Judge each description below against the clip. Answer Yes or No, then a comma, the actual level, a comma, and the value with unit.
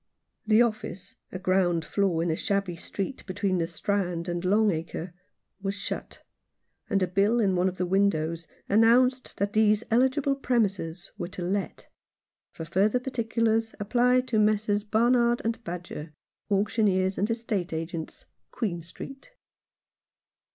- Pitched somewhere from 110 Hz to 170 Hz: No, high, 200 Hz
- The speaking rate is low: No, average, 145 wpm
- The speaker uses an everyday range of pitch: Yes, average, 4.1 semitones